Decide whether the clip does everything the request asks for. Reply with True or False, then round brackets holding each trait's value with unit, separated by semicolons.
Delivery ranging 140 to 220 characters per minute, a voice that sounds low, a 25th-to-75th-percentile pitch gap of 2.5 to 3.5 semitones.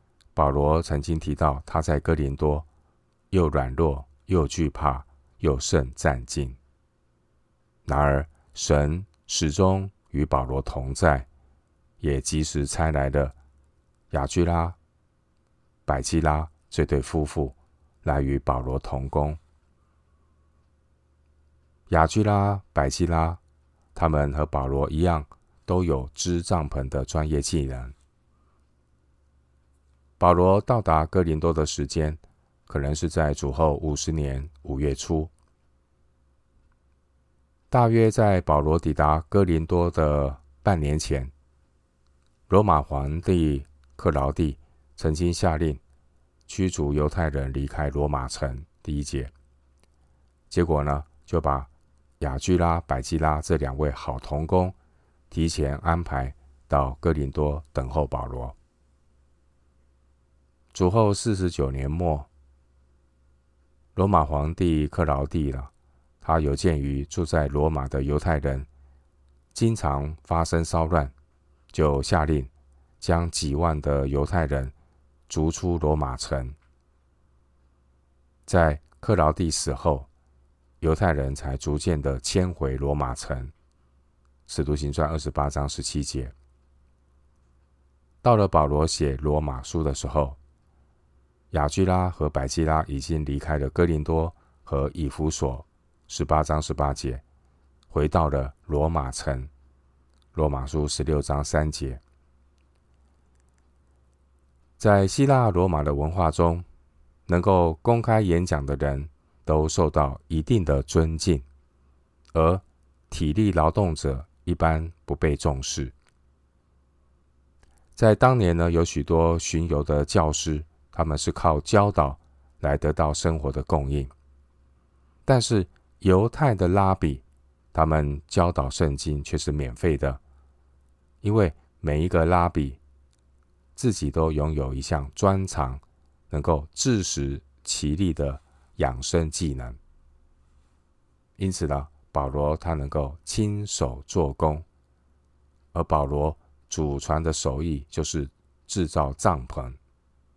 True (170 characters per minute; 75 Hz; 3.1 semitones)